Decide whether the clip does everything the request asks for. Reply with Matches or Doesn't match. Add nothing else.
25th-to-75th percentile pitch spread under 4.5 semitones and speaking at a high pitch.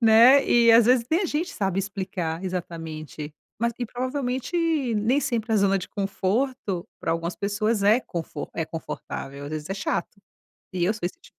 Doesn't match